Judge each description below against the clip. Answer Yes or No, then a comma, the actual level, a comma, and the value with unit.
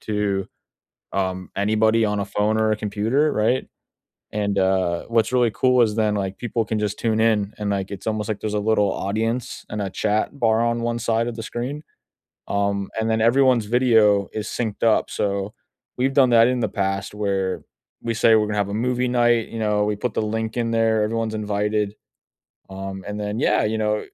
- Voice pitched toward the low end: Yes, low, 110 Hz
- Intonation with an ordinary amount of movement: No, narrow, 2.1 semitones